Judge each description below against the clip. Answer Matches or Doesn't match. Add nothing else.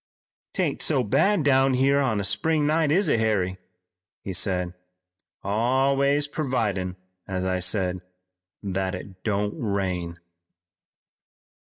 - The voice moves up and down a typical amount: Doesn't match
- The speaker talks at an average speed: Doesn't match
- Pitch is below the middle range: Matches